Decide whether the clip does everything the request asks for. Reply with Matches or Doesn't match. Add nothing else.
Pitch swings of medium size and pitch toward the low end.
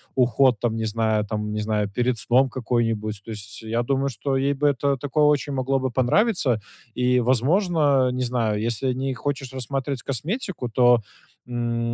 Matches